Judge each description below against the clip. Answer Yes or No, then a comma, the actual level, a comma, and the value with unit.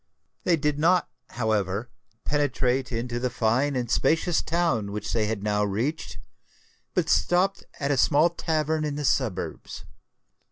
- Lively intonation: Yes, wide, 5.7 semitones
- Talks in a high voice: No, low, 130 Hz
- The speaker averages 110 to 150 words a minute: Yes, average, 145 wpm